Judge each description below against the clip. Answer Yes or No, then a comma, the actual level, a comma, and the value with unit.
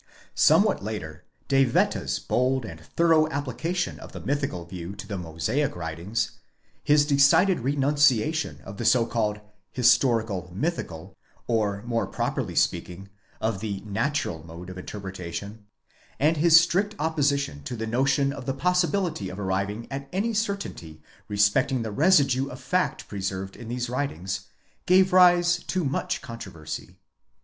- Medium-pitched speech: No, low, 120 Hz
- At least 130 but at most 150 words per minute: Yes, average, 140 wpm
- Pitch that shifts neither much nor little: No, wide, 7.1 semitones